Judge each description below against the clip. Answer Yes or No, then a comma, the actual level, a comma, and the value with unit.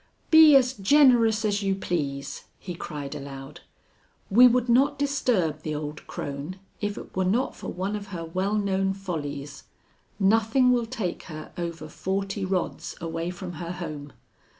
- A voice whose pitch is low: No, high, 190 Hz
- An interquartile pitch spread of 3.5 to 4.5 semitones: No, wide, 5.6 semitones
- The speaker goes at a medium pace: Yes, average, 155 wpm